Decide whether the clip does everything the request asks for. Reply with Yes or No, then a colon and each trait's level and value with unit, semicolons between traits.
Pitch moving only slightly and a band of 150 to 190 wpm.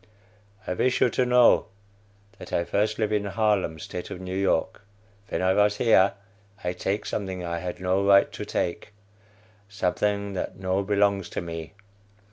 Yes: narrow, 2.3 semitones; average, 165 wpm